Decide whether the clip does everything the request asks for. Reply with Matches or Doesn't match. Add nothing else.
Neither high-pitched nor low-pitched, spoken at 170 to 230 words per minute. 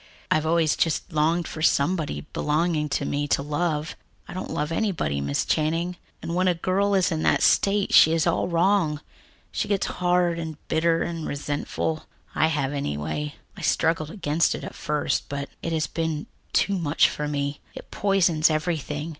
Matches